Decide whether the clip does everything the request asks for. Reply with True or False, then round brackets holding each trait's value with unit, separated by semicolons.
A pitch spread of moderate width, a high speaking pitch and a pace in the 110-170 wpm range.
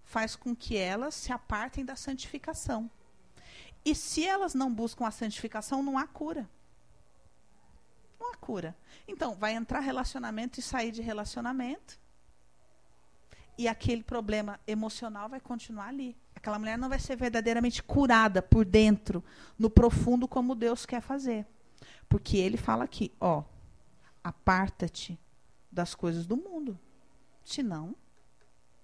True (4.1 semitones; 230 Hz; 130 wpm)